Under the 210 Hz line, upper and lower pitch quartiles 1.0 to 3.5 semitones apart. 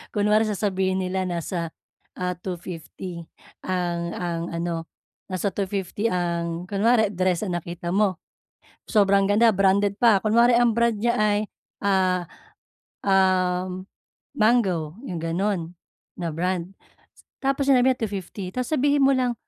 Yes: high, 190 Hz; average, 3.2 semitones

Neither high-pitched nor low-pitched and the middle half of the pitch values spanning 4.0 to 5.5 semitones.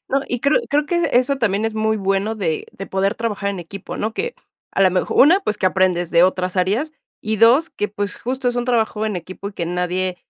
No: high, 210 Hz; average, 4.5 semitones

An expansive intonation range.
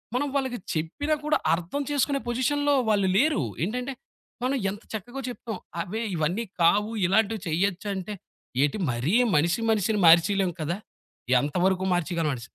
Yes: wide, 6.3 semitones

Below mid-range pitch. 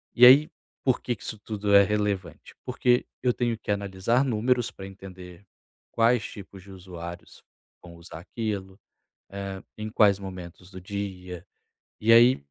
Yes: low, 100 Hz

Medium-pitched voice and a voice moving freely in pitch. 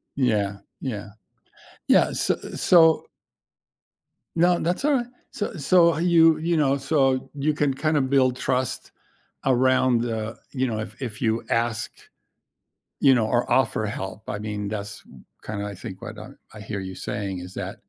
No: low, 130 Hz; wide, 5.9 semitones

